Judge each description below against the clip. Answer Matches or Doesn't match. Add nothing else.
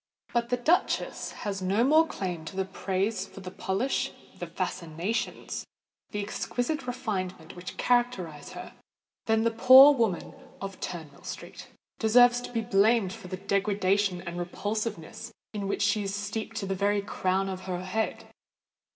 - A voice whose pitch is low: Doesn't match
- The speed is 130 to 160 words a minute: Matches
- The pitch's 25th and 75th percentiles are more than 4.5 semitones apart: Doesn't match